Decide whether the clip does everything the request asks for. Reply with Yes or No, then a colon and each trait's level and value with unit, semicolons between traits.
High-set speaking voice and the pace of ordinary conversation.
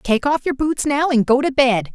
No: very high, 270 Hz; fast, 280 wpm